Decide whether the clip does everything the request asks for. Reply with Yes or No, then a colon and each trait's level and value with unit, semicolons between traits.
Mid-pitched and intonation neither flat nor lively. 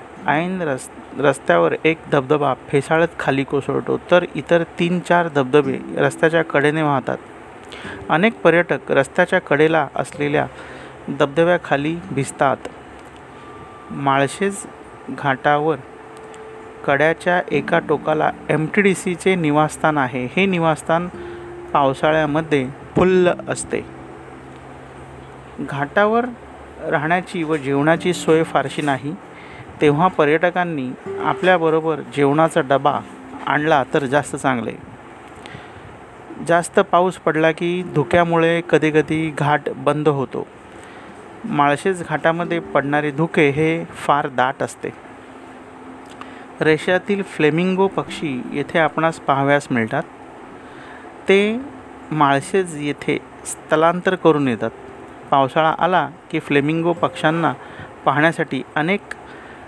Yes: medium, 160 Hz; average, 3.1 semitones